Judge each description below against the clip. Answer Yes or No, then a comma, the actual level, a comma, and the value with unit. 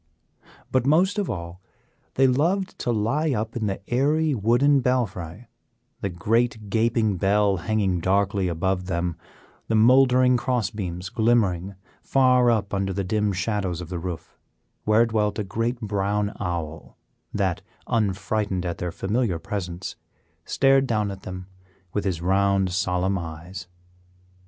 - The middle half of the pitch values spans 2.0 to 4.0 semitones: No, average, 4.4 semitones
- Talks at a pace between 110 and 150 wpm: Yes, average, 140 wpm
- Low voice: Yes, low, 100 Hz